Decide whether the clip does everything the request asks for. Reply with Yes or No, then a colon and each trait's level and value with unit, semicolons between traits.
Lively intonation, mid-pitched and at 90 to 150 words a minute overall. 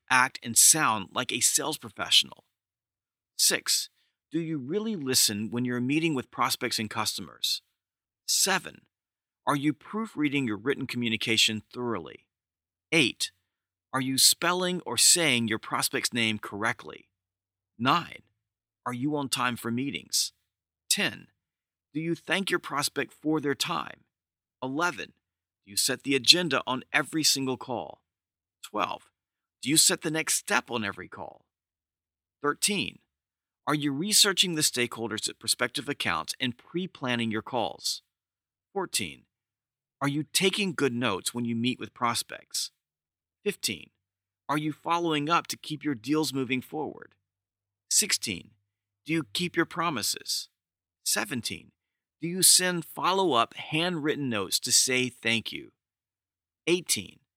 No: wide, 6.2 semitones; low, 125 Hz; slow, 135 wpm